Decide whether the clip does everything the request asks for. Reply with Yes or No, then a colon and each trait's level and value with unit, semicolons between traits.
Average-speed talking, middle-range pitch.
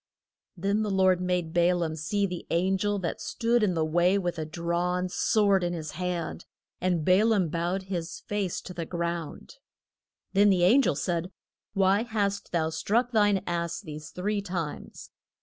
Yes: average, 175 wpm; medium, 180 Hz